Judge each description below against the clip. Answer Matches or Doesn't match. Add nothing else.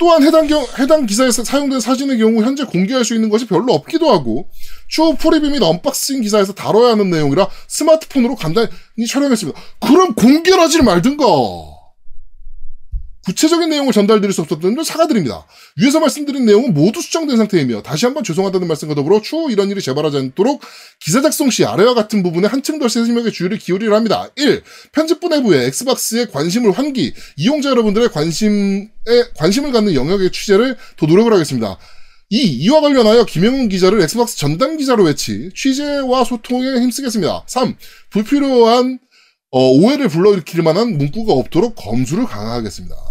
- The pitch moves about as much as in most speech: Doesn't match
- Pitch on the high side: Matches